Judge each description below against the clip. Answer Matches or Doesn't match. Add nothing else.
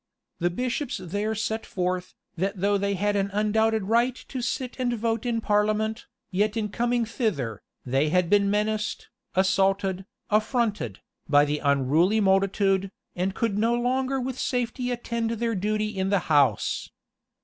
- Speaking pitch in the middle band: Doesn't match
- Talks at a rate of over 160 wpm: Doesn't match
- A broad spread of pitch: Doesn't match